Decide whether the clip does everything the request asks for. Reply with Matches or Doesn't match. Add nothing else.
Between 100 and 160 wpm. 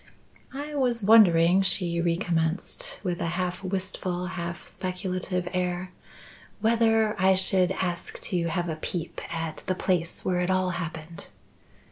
Matches